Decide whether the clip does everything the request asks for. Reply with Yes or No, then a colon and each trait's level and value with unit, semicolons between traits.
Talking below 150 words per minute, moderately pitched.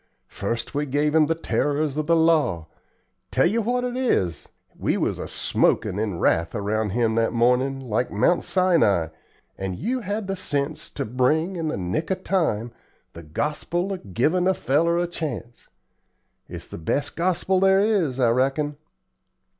No: average, 170 wpm; medium, 150 Hz